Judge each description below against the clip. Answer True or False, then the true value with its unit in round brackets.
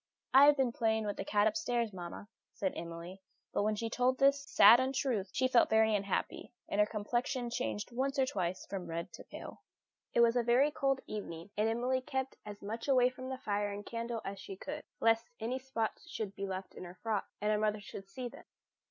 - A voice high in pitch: True (225 Hz)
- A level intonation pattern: False (4.0 semitones)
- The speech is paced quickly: True (215 wpm)